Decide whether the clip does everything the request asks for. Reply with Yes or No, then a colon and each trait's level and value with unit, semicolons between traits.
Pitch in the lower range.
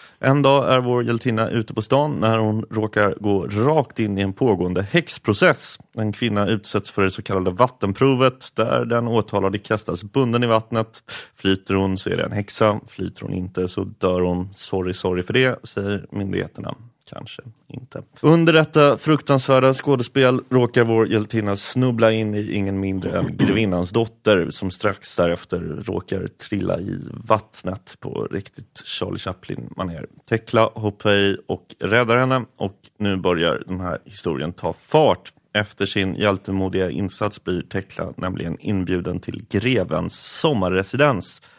Yes: low, 110 Hz